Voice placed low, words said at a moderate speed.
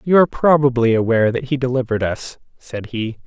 Yes: low, 125 Hz; average, 185 wpm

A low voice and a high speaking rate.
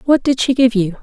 No: high, 240 Hz; fast, 290 wpm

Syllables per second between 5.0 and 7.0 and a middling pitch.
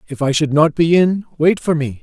Yes: 5.1 syllables/s; medium, 155 Hz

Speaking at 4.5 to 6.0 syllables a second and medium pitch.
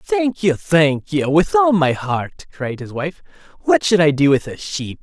No: 4.2 syllables/s; medium, 160 Hz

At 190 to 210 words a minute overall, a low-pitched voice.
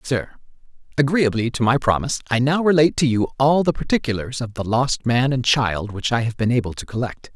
Yes: fast, 205 wpm; low, 125 Hz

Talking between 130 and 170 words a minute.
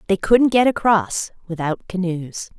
Yes: average, 140 wpm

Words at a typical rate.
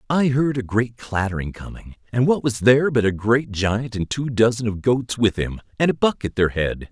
No: fast, 235 wpm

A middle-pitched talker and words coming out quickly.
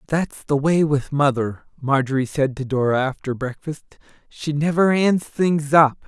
No: medium, 145 Hz; average, 160 wpm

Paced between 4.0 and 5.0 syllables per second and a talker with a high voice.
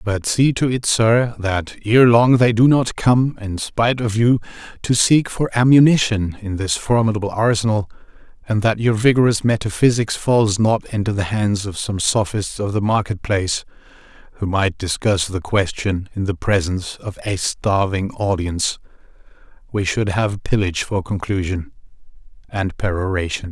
No: 4.7 syllables/s; low, 105 Hz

